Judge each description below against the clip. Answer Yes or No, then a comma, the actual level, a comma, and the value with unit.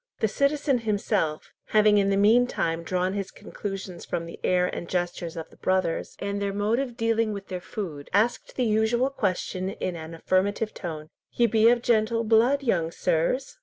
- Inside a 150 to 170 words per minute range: No, average, 180 wpm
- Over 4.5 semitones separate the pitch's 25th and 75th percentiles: No, average, 4.1 semitones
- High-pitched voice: Yes, high, 200 Hz